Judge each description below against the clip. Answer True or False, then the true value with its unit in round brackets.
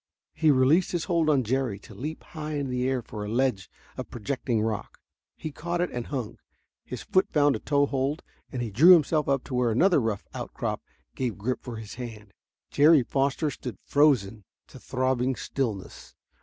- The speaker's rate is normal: True (185 wpm)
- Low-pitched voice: True (130 Hz)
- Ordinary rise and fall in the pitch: True (4.3 semitones)